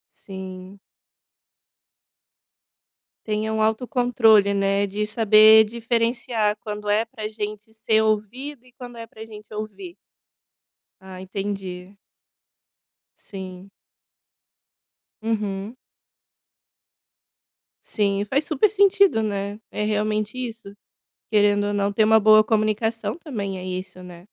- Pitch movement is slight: Yes, narrow, 2.1 semitones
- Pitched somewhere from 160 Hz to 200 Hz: No, high, 215 Hz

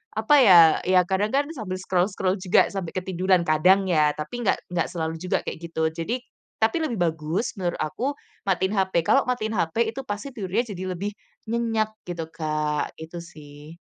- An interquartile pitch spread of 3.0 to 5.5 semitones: Yes, average, 4.6 semitones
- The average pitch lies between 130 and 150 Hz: No, medium, 185 Hz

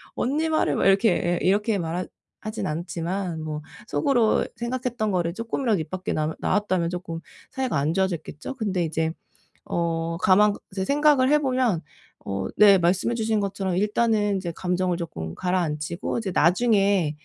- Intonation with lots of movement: No, average, 4.8 semitones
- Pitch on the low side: No, high, 190 Hz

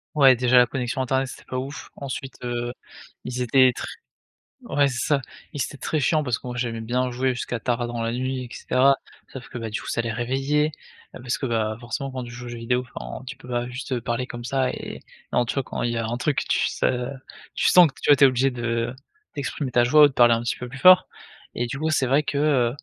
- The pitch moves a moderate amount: No, narrow, 2.1 semitones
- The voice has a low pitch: Yes, low, 125 Hz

